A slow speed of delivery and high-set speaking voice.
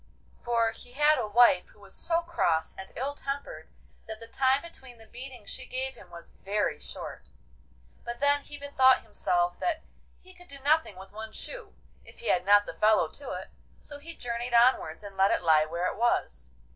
No: average, 200 wpm; high, 240 Hz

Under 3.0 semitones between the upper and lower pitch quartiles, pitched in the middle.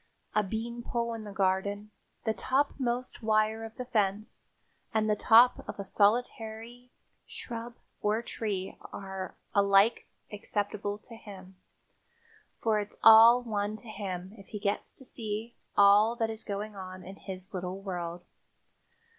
No: narrow, 2.4 semitones; high, 210 Hz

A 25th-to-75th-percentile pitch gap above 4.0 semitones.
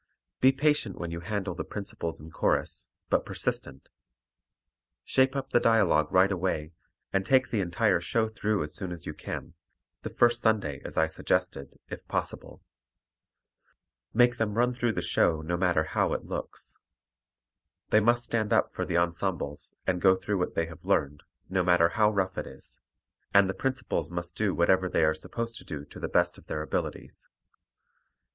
Yes: average, 5.0 semitones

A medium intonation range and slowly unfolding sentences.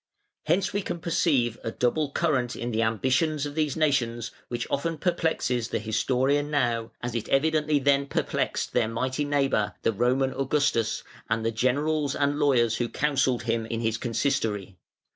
No: average, 4.0 semitones; average, 160 wpm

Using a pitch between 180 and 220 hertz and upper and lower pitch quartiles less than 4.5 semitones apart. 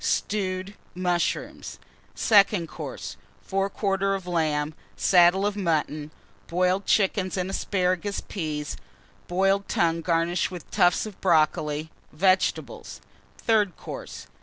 Yes: medium, 185 Hz; average, 2.7 semitones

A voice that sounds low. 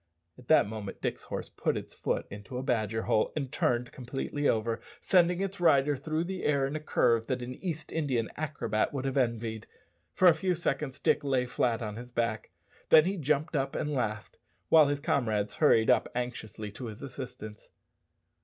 Yes: low, 130 Hz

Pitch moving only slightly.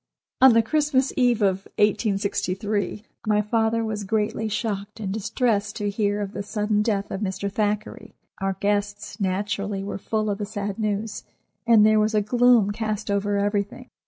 Yes: narrow, 1.5 semitones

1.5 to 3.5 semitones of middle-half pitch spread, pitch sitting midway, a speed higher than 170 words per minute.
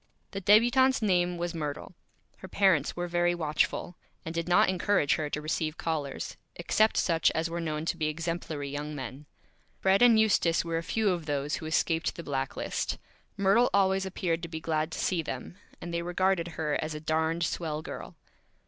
Yes: average, 3.2 semitones; medium, 165 Hz; average, 190 wpm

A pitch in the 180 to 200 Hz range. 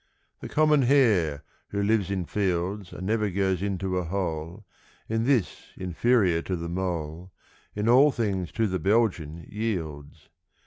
No: very low, 95 Hz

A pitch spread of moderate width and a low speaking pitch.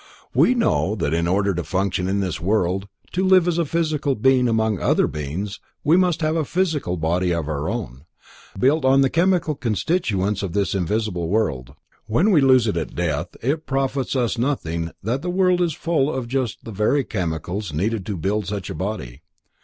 No: wide, 7.9 semitones; low, 110 Hz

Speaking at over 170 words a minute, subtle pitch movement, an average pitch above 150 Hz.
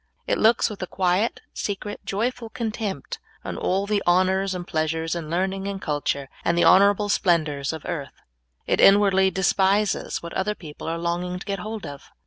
No: average, 180 wpm; average, 3.1 semitones; high, 190 Hz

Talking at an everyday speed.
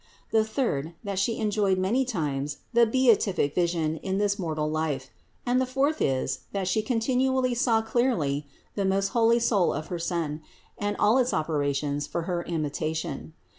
Yes: average, 165 wpm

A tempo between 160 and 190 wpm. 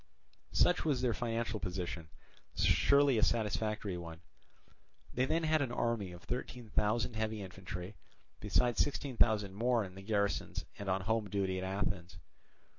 No: average, 145 wpm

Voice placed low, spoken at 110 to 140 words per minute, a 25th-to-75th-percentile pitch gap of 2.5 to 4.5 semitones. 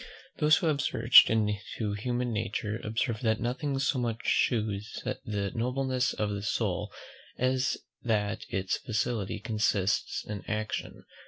Yes: low, 110 Hz; slow, 135 wpm; average, 3.3 semitones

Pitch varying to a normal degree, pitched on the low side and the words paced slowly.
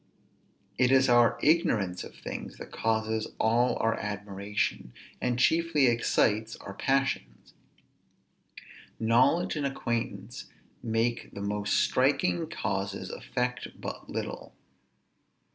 Yes: average, 3.5 semitones; low, 115 Hz; slow, 105 wpm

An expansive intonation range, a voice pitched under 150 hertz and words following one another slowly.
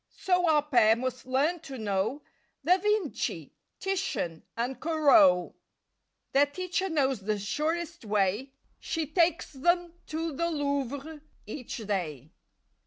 No: wide, 6.4 semitones; very high, 285 Hz; slow, 120 wpm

